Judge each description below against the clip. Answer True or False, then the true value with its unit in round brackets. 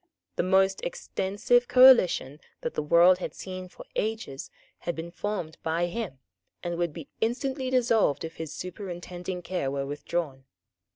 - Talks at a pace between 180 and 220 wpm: False (150 wpm)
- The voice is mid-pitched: True (180 Hz)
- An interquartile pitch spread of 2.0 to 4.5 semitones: False (4.9 semitones)